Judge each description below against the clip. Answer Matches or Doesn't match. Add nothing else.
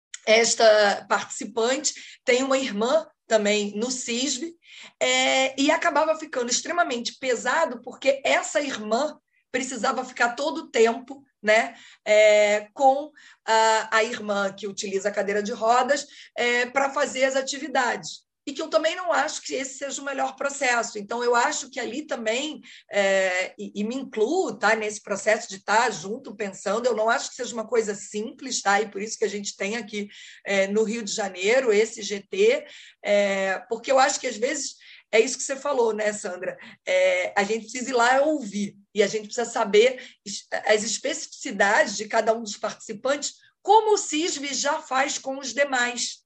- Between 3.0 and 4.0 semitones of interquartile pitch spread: Doesn't match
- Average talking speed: Matches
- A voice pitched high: Matches